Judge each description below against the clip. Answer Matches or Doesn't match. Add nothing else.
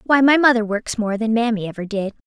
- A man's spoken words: Doesn't match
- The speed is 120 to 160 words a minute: Doesn't match